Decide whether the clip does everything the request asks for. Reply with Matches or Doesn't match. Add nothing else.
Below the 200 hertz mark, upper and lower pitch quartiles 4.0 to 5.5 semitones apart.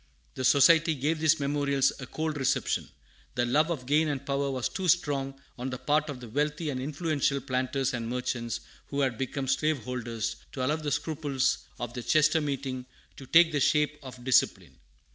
Doesn't match